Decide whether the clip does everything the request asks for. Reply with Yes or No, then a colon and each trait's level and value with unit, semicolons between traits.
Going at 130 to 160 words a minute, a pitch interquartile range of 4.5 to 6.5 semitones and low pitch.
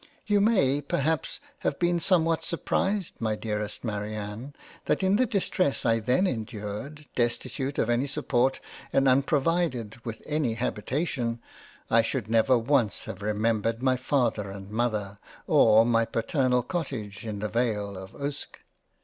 Yes: average, 140 wpm; average, 4.9 semitones; low, 120 Hz